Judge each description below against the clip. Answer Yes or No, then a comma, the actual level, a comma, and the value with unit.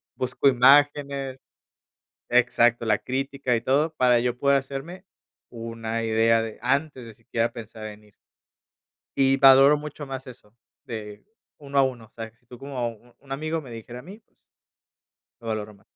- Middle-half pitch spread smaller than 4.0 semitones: Yes, average, 3.3 semitones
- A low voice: Yes, low, 125 Hz